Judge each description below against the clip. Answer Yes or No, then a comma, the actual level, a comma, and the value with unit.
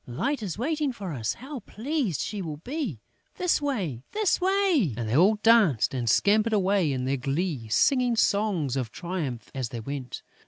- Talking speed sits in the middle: Yes, average, 180 wpm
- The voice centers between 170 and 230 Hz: Yes, high, 190 Hz